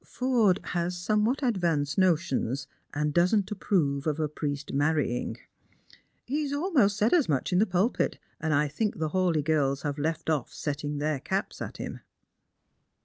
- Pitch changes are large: Yes, wide, 5.9 semitones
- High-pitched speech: No, medium, 165 Hz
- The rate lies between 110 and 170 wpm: Yes, average, 160 wpm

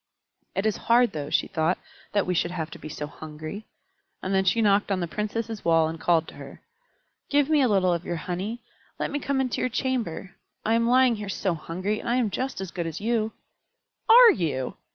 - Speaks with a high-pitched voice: Yes, high, 200 Hz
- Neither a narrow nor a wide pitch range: No, wide, 5.7 semitones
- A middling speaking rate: No, fast, 220 wpm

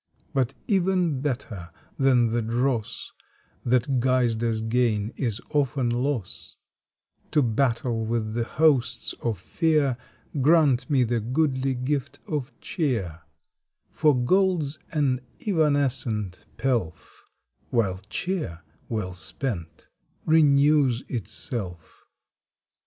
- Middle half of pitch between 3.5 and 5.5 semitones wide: Yes, average, 4.2 semitones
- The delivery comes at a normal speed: No, slow, 100 wpm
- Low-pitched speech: Yes, low, 125 Hz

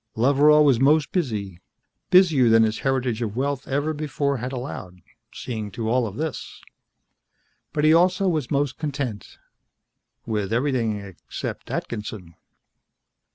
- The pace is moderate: No, slow, 130 wpm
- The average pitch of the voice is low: Yes, low, 130 Hz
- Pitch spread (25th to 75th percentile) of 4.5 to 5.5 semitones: Yes, average, 4.9 semitones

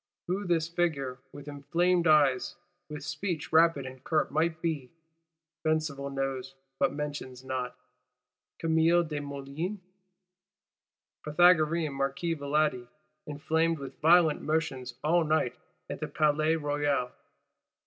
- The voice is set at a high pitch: No, medium, 150 Hz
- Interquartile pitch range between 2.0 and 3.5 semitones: Yes, average, 2.9 semitones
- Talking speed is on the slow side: Yes, slow, 110 wpm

